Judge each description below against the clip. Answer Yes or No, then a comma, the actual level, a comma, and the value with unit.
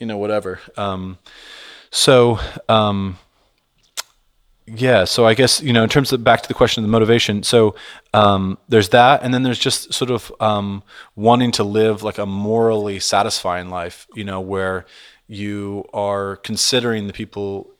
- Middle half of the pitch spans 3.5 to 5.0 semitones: No, average, 2.8 semitones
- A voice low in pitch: Yes, low, 105 Hz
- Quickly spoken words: No, average, 165 wpm